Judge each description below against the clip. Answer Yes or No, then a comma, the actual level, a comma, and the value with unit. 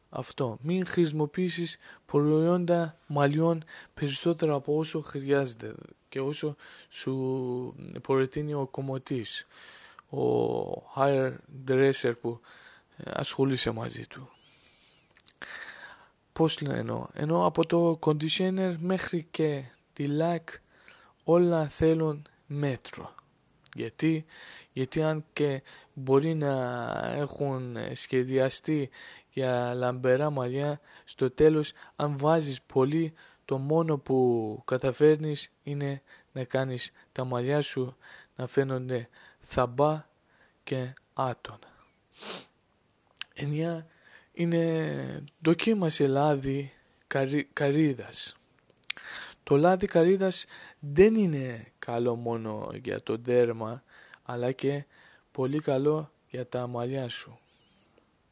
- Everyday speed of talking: No, slow, 95 wpm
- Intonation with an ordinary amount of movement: Yes, average, 3.3 semitones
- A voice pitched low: No, medium, 145 Hz